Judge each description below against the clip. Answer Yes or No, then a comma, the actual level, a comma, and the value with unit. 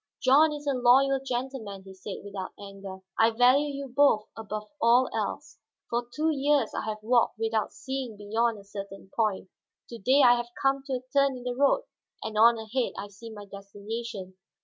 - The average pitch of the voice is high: Yes, high, 235 Hz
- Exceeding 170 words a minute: Yes, average, 190 wpm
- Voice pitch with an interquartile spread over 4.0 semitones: Yes, average, 4.5 semitones